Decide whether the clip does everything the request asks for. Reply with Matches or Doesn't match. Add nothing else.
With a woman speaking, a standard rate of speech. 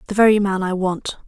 Doesn't match